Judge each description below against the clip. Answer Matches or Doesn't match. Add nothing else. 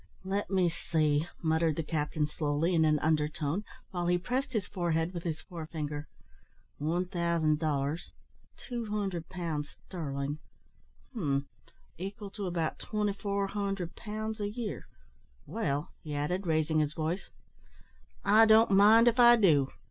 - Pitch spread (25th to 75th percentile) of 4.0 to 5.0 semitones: Matches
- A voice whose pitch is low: Doesn't match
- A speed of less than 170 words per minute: Matches